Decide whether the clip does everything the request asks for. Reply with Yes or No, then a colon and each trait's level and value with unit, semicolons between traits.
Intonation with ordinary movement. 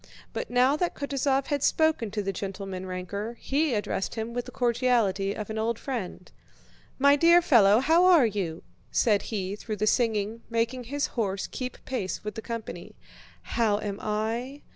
Yes: average, 4.2 semitones